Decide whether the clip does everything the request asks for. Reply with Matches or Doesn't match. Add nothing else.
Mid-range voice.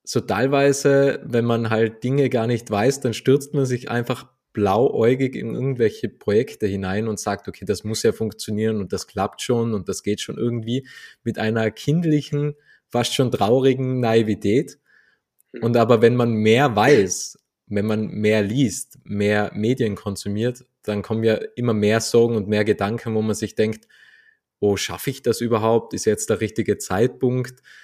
Doesn't match